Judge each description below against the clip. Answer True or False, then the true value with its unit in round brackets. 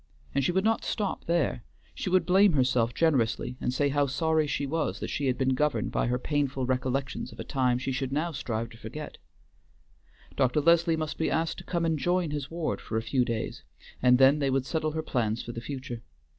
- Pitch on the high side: False (140 Hz)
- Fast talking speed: True (220 wpm)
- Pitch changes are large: False (4.2 semitones)